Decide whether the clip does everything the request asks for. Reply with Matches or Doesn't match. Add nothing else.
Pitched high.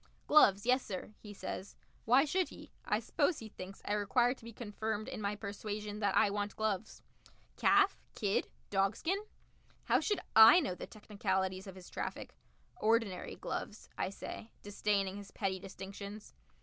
Matches